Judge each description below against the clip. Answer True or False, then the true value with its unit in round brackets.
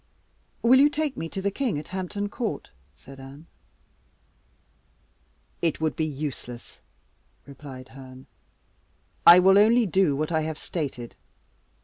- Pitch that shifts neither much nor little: False (6.5 semitones)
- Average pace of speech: False (130 wpm)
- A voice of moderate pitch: True (160 Hz)